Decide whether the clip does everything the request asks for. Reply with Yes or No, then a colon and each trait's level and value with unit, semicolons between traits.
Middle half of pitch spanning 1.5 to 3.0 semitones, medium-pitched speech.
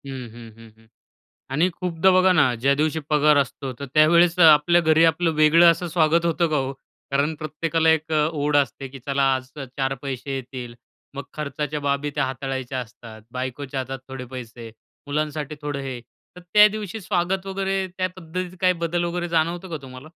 No: average, 4.1 semitones; medium, 150 Hz